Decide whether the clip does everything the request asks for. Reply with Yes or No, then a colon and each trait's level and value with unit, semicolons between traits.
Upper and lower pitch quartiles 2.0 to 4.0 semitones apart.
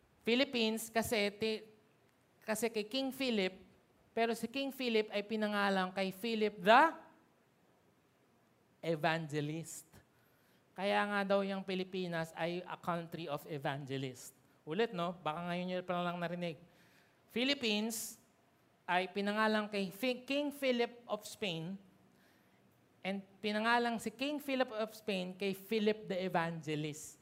No: average, 4.4 semitones